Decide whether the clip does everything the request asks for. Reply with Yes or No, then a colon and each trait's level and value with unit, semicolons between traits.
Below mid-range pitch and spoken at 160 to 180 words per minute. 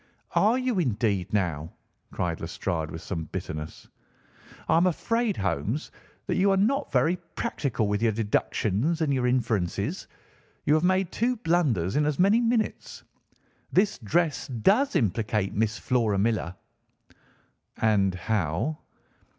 No: low, 115 Hz; slow, 135 wpm